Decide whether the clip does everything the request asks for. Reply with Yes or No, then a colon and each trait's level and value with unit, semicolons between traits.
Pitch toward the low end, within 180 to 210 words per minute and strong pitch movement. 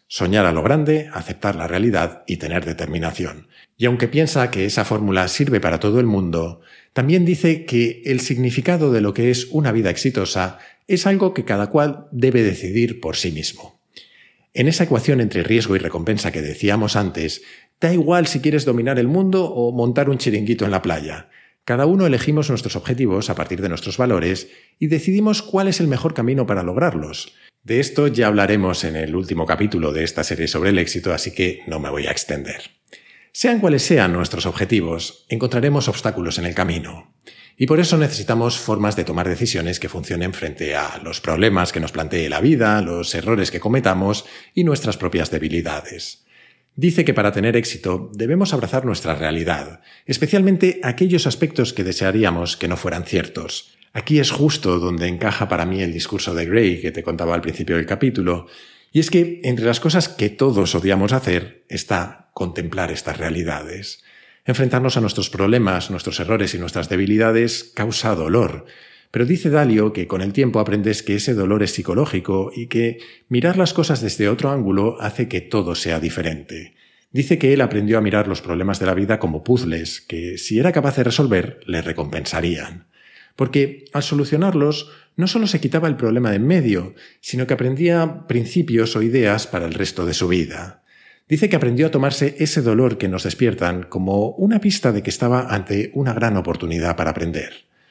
Yes: low, 110 Hz; average, 185 wpm; wide, 7.1 semitones